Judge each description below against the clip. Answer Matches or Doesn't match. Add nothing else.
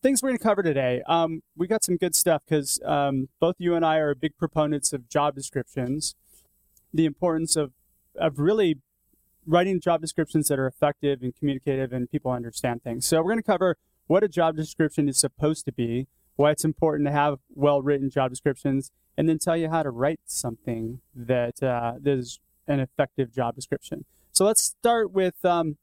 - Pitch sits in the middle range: Matches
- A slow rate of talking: Doesn't match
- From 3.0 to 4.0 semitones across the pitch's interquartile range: Matches